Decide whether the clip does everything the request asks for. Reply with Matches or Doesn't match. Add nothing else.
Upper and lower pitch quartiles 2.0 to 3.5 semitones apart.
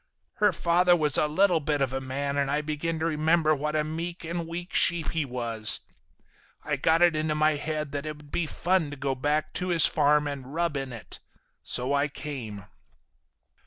Matches